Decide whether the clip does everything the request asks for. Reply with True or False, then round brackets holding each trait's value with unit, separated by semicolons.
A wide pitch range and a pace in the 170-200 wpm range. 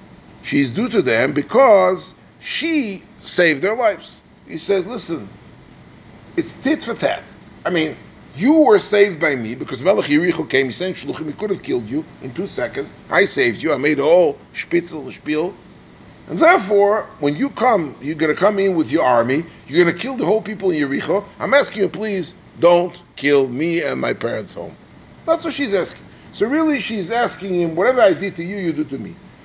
True (7.8 semitones; 195 wpm)